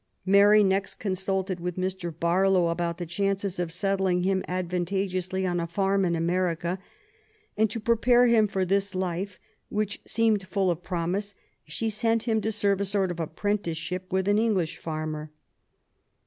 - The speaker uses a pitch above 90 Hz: Yes, high, 190 Hz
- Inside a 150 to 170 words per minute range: Yes, average, 160 wpm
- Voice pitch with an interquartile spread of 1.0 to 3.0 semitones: Yes, narrow, 2.4 semitones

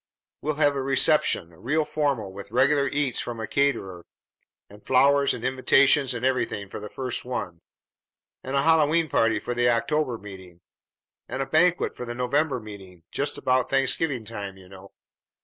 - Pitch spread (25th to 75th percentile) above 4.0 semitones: Yes, average, 5.1 semitones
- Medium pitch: No, low, 125 Hz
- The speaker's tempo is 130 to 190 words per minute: Yes, average, 165 wpm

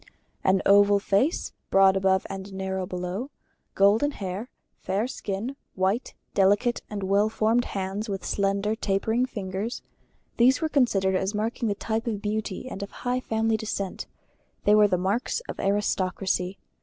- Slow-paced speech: No, average, 150 wpm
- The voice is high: Yes, high, 200 Hz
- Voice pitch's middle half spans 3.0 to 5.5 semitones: No, narrow, 2.6 semitones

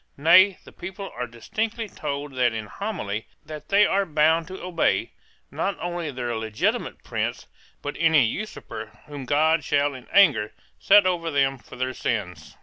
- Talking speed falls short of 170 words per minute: Yes, average, 160 wpm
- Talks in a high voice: No, medium, 150 Hz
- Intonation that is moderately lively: No, wide, 6.7 semitones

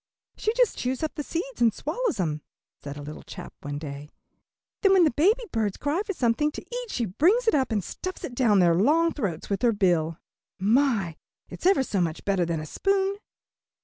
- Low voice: No, high, 240 Hz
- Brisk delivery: Yes, fast, 210 wpm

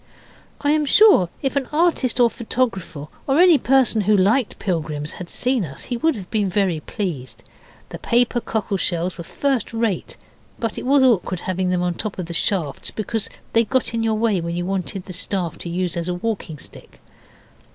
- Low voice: No, high, 200 Hz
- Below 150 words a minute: No, fast, 205 wpm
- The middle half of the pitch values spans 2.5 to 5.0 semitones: No, wide, 5.4 semitones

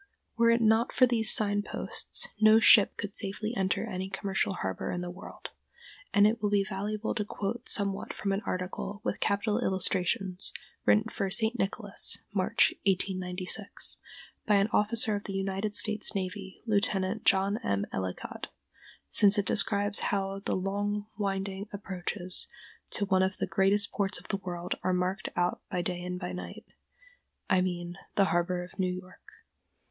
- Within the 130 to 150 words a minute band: No, average, 165 wpm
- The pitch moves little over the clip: Yes, narrow, 2.1 semitones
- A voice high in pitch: Yes, high, 195 Hz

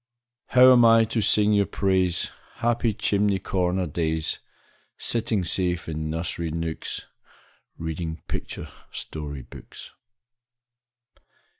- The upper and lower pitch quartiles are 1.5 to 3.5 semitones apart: No, average, 4.6 semitones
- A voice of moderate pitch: No, very low, 90 Hz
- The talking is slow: Yes, slow, 105 wpm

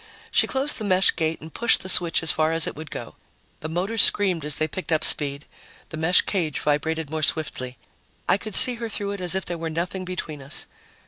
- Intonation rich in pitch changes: No, average, 3.3 semitones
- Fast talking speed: Yes, fast, 230 wpm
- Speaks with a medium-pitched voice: Yes, medium, 165 Hz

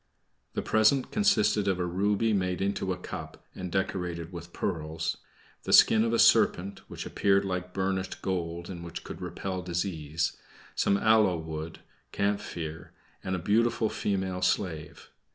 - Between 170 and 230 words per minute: No, average, 150 wpm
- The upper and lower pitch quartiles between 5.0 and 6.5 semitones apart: No, average, 2.8 semitones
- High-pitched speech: No, very low, 95 Hz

